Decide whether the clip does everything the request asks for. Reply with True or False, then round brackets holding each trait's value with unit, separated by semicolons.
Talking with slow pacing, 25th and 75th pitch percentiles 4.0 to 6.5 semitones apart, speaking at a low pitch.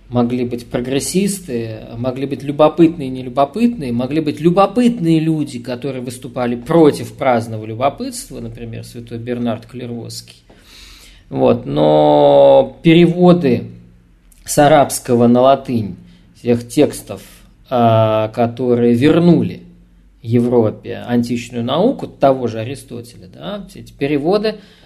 True (100 wpm; 4.4 semitones; 120 Hz)